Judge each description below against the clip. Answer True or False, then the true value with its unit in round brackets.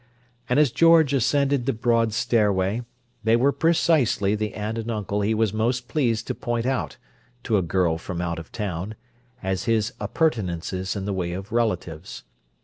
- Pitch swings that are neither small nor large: True (4.4 semitones)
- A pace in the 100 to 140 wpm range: False (170 wpm)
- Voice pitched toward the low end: True (110 Hz)